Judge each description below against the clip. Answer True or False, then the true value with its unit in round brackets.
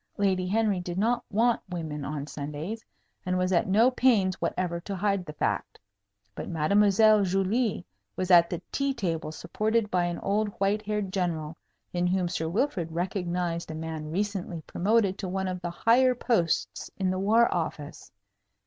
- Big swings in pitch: False (3.6 semitones)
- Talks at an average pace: True (165 wpm)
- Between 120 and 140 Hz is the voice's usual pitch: False (185 Hz)